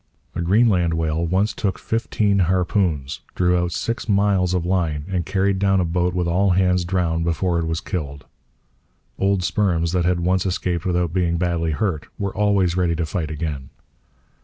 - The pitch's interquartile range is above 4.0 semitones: No, narrow, 2.4 semitones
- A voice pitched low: Yes, very low, 90 Hz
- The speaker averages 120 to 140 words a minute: No, average, 175 wpm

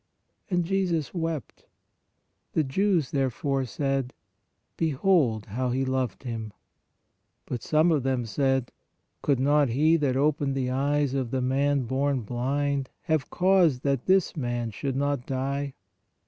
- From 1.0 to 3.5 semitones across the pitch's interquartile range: Yes, average, 2.7 semitones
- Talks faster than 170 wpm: No, slow, 135 wpm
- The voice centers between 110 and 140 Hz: Yes, low, 135 Hz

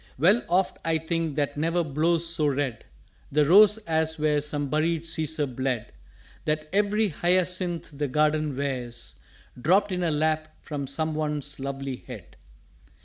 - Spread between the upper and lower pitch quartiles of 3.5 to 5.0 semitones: No, average, 2.8 semitones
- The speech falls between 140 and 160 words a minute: Yes, average, 150 wpm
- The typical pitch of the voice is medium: Yes, medium, 155 Hz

